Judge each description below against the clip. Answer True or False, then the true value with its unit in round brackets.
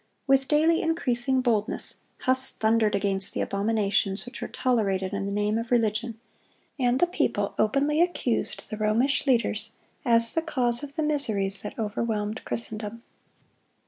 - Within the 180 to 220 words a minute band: False (145 wpm)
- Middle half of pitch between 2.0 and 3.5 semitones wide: False (4.0 semitones)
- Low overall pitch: False (230 Hz)